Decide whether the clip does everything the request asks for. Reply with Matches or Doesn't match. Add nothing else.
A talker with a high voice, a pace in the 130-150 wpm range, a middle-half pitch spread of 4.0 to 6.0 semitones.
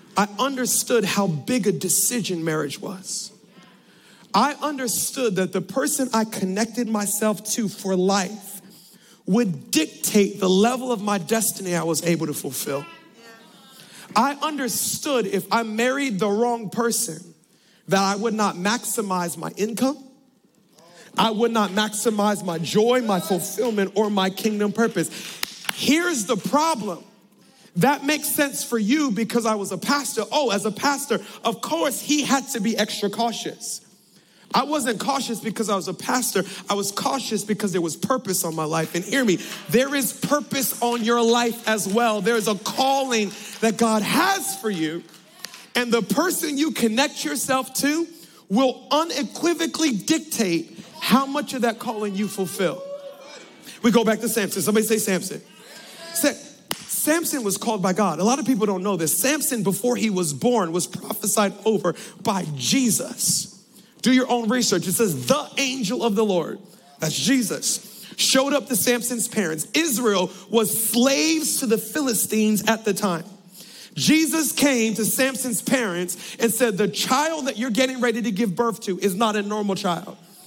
Doesn't match